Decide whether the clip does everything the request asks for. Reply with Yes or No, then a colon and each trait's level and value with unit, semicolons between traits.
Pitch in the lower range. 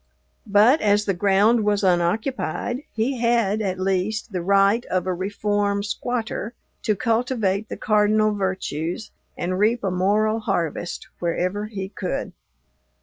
No: high, 205 Hz